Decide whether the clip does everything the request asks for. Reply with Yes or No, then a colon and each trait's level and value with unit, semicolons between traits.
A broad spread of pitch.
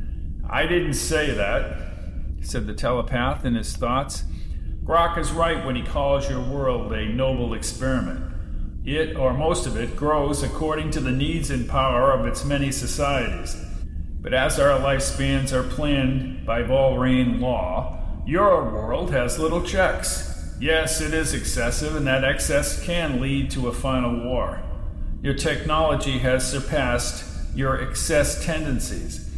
Yes: wide, 8.6 semitones